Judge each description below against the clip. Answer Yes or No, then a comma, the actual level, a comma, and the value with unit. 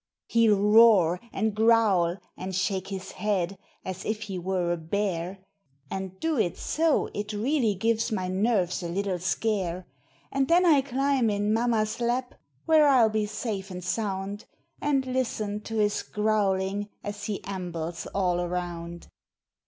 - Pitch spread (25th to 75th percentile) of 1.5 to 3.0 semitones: No, average, 3.4 semitones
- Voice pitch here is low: No, high, 205 Hz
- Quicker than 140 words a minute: Yes, average, 150 wpm